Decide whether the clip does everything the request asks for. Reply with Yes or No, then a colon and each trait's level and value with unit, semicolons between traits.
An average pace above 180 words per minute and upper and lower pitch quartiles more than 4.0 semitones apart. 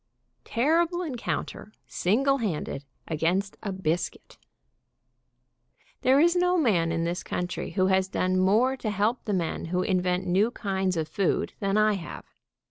No: average, 145 wpm; average, 5.0 semitones